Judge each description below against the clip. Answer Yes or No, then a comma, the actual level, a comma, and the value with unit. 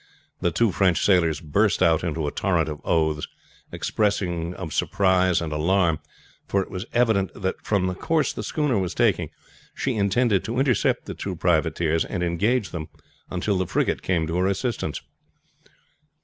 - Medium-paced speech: Yes, average, 165 wpm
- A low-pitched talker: Yes, very low, 90 Hz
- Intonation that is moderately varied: Yes, average, 3.6 semitones